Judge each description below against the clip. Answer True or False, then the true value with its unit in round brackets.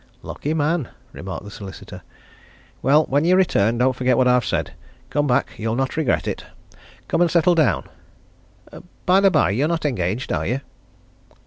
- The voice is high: False (135 Hz)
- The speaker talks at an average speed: True (170 wpm)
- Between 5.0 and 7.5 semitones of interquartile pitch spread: True (5.4 semitones)